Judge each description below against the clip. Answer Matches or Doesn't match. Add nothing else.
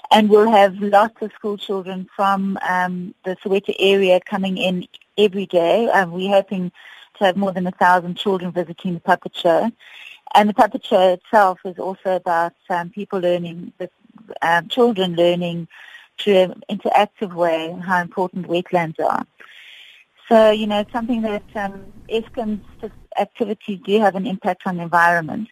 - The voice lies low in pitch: Doesn't match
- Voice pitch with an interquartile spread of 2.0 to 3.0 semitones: Matches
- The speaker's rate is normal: Matches